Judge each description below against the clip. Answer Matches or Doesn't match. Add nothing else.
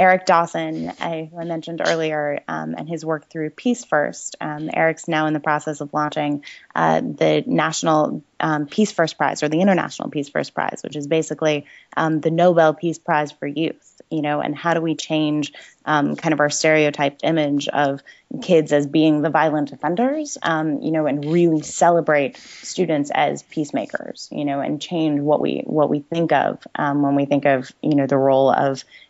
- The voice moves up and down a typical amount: Doesn't match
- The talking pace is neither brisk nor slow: Matches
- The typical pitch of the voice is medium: Matches